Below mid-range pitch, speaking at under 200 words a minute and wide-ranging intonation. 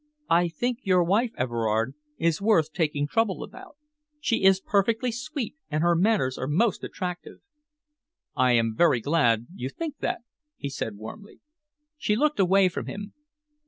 No: medium, 180 Hz; average, 155 wpm; wide, 7.8 semitones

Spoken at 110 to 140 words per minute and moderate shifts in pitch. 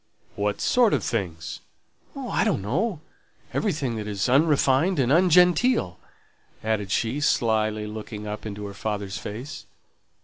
No: slow, 135 wpm; wide, 6.4 semitones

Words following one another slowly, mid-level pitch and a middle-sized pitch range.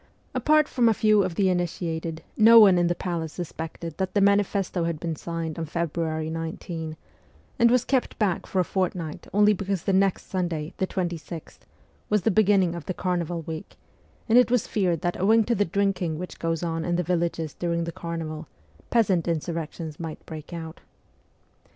No: average, 185 wpm; medium, 175 Hz; average, 3.2 semitones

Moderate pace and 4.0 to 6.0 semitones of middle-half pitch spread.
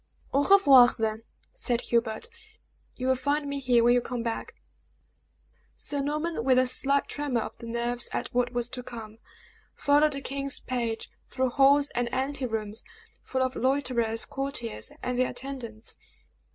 No: average, 155 wpm; average, 2.8 semitones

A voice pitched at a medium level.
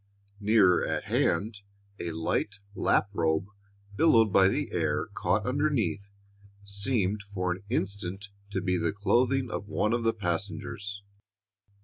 No: low, 100 Hz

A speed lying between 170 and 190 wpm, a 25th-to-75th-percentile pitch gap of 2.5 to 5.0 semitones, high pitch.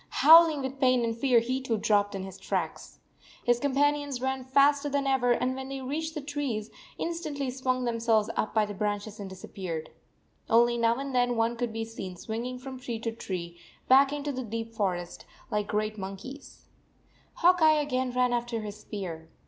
No: average, 200 wpm; average, 4.1 semitones; high, 245 Hz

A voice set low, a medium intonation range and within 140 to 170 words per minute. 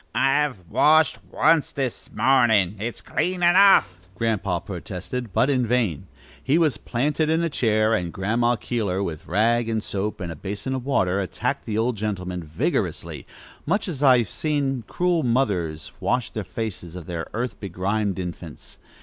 No: low, 110 Hz; wide, 6.2 semitones; average, 160 wpm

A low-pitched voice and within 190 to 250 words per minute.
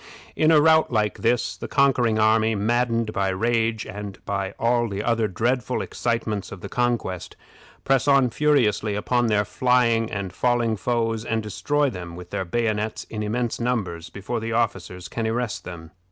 No: low, 115 Hz; average, 170 wpm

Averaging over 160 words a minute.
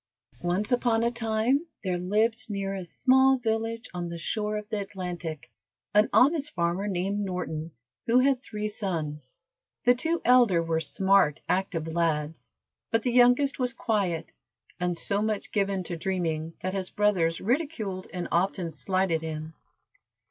No: average, 150 wpm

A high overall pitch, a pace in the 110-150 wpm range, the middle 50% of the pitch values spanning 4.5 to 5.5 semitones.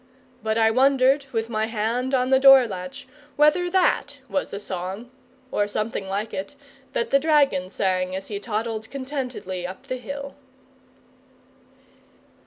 Yes: high, 235 Hz; average, 145 wpm; average, 5.1 semitones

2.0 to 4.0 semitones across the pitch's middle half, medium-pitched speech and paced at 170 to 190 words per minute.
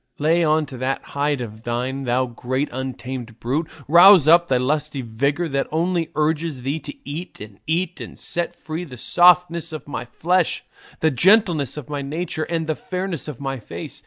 No: average, 4.4 semitones; medium, 150 Hz; average, 185 wpm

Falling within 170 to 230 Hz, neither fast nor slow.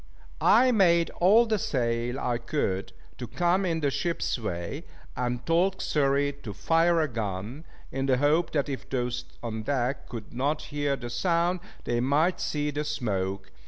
No: medium, 140 Hz; average, 165 wpm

